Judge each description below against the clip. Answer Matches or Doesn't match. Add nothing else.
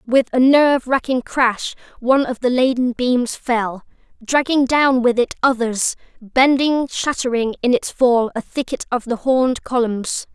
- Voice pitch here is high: Matches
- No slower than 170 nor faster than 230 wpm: Doesn't match